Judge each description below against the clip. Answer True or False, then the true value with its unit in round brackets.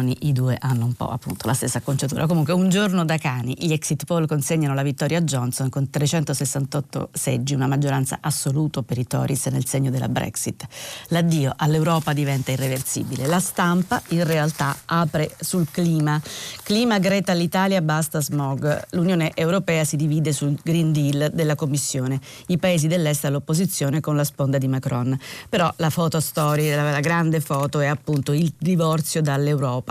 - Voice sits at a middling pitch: True (150 Hz)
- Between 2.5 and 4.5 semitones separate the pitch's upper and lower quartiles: True (3.0 semitones)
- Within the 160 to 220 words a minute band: True (165 wpm)